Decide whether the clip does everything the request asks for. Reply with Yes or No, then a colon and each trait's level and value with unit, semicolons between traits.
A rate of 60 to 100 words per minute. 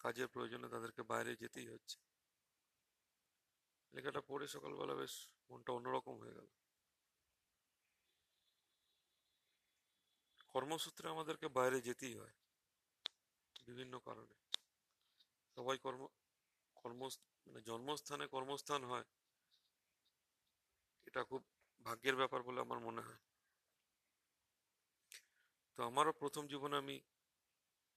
Yes: average, 85 wpm